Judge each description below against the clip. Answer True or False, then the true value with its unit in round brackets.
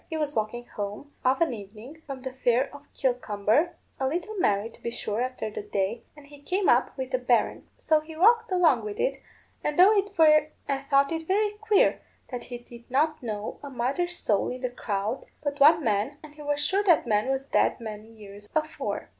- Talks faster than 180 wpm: True (200 wpm)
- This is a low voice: False (270 Hz)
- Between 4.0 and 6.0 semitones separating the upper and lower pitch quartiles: True (5.2 semitones)